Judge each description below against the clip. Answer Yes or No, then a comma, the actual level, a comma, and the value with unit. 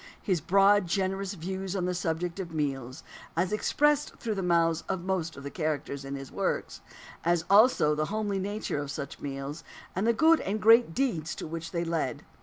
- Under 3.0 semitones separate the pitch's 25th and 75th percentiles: No, average, 4.3 semitones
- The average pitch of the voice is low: No, medium, 175 Hz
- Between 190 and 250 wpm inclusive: Yes, average, 195 wpm